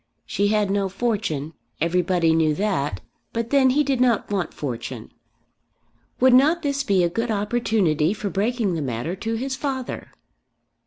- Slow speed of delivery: No, average, 155 wpm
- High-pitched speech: Yes, high, 205 Hz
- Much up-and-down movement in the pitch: Yes, wide, 6.4 semitones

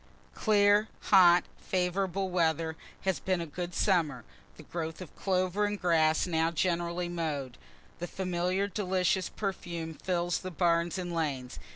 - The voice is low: No, medium, 175 Hz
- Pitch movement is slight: Yes, narrow, 2.2 semitones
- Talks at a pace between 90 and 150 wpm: Yes, average, 145 wpm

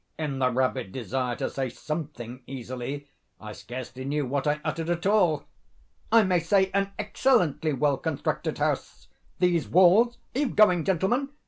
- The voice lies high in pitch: No, medium, 150 Hz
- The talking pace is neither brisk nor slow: Yes, average, 145 wpm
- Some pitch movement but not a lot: No, wide, 6.5 semitones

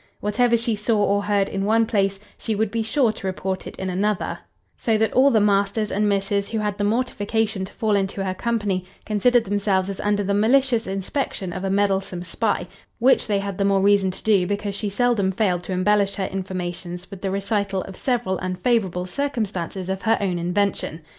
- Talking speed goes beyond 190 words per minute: Yes, average, 200 wpm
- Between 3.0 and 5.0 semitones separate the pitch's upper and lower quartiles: No, narrow, 2.4 semitones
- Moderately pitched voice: No, high, 200 Hz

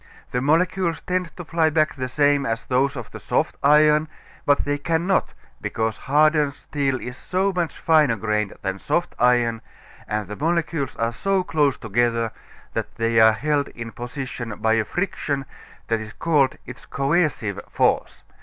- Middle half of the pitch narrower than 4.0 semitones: No, wide, 5.5 semitones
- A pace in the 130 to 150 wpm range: No, average, 165 wpm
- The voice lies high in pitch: No, medium, 140 Hz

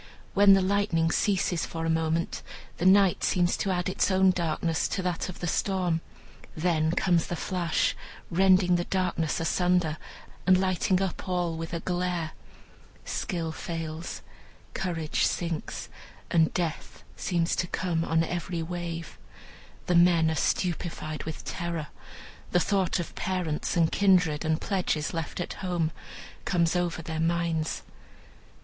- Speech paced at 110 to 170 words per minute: Yes, average, 140 wpm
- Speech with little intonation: Yes, narrow, 1.9 semitones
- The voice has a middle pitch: Yes, medium, 175 Hz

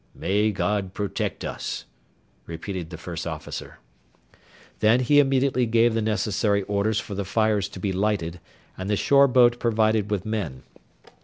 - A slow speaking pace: No, average, 150 wpm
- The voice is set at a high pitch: No, low, 105 Hz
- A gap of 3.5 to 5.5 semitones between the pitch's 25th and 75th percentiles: No, average, 2.9 semitones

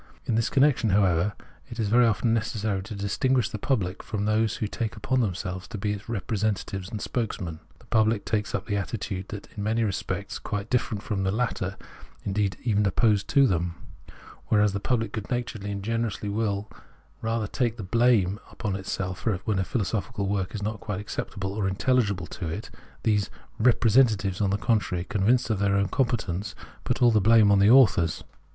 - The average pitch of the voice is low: Yes, low, 105 Hz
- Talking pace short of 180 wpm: No, average, 185 wpm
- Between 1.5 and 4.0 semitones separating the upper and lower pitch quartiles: Yes, average, 2.7 semitones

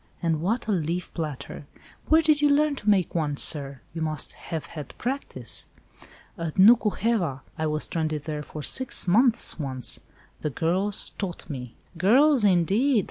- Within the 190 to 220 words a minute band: No, average, 160 wpm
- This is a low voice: No, medium, 175 Hz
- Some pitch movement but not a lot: No, wide, 6.9 semitones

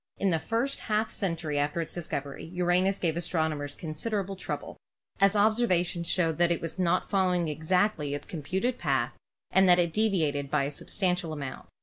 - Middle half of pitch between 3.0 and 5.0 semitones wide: Yes, average, 3.8 semitones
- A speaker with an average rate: Yes, average, 175 wpm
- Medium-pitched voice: Yes, medium, 175 Hz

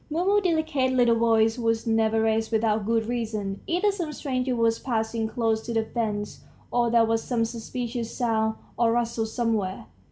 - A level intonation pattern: Yes, narrow, 1.8 semitones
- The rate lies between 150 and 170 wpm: Yes, average, 165 wpm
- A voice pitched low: No, high, 230 Hz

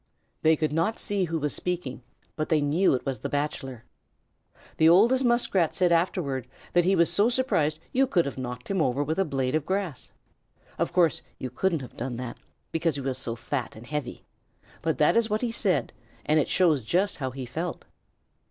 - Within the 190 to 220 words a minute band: Yes, average, 200 wpm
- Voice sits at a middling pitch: Yes, medium, 155 Hz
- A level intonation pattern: No, wide, 5.5 semitones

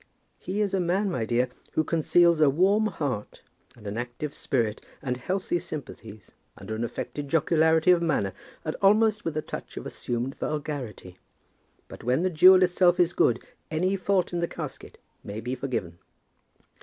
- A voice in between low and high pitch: Yes, medium, 155 Hz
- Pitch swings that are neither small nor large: No, wide, 6.7 semitones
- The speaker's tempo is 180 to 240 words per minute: No, average, 170 wpm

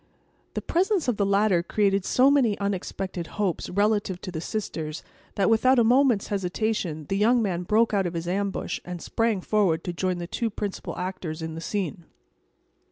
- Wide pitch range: No, average, 3.6 semitones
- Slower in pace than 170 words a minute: No, average, 180 wpm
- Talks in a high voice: Yes, high, 200 Hz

